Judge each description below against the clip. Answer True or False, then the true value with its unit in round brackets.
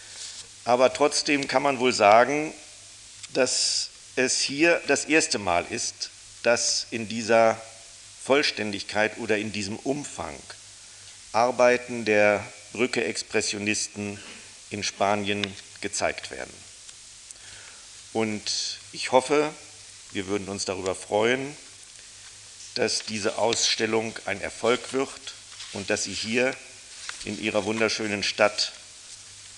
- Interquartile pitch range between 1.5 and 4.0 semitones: True (3.2 semitones)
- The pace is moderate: False (100 wpm)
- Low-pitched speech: True (110 Hz)